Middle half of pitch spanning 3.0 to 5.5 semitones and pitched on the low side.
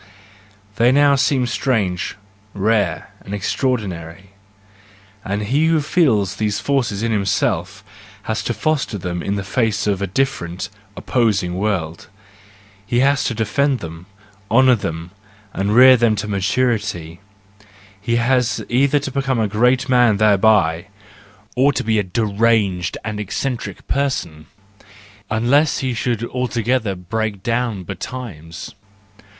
Yes: average, 4.5 semitones; low, 110 Hz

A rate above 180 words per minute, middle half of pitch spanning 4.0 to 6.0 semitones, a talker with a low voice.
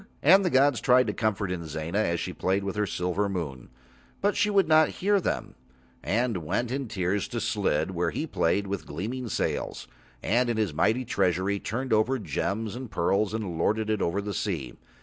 Yes: average, 190 wpm; wide, 5.6 semitones; low, 105 Hz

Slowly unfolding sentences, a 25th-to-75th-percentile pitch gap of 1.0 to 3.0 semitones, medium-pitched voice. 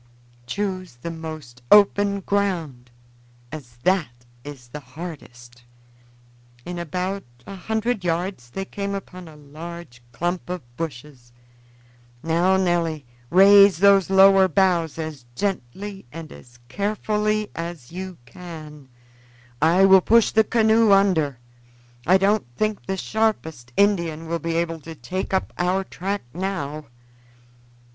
No: slow, 125 wpm; average, 4.4 semitones; medium, 175 Hz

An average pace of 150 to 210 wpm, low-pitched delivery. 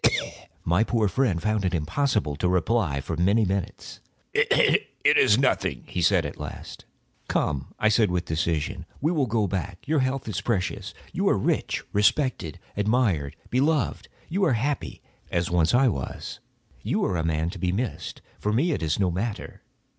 Yes: average, 170 wpm; low, 100 Hz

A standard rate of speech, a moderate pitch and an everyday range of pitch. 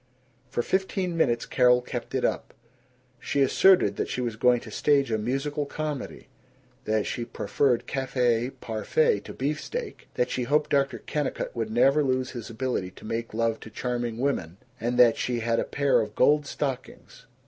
No: average, 170 wpm; low, 125 Hz; average, 3.4 semitones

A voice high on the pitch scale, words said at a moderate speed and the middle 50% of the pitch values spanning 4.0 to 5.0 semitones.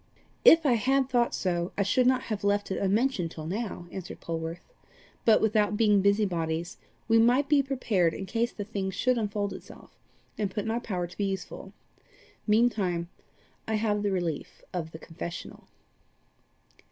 Yes: high, 205 Hz; average, 170 wpm; average, 4.4 semitones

